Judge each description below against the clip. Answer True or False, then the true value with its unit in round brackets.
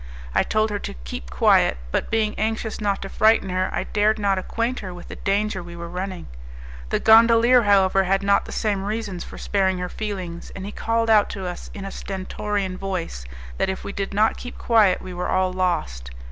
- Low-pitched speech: False (195 Hz)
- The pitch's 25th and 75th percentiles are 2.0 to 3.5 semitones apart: True (2.6 semitones)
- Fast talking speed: True (210 wpm)